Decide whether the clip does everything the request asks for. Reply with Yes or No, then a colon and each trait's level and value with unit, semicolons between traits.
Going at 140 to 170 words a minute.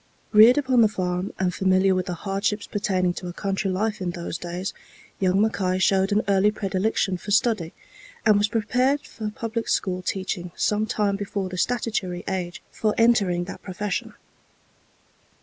Yes: average, 165 wpm